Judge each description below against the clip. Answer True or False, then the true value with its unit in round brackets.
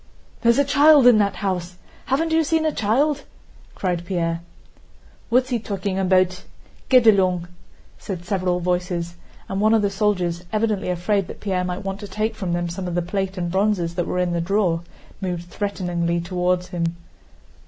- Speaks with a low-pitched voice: False (190 Hz)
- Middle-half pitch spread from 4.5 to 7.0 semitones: False (3.3 semitones)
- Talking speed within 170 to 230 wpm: True (175 wpm)